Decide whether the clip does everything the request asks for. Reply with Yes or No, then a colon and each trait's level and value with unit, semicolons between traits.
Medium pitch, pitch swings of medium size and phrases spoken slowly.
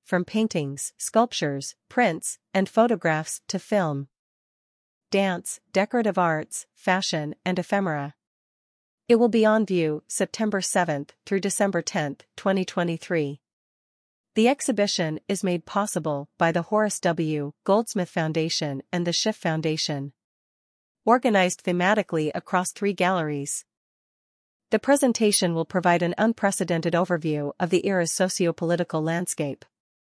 Yes: medium, 180 Hz; average, 4.3 semitones; slow, 115 wpm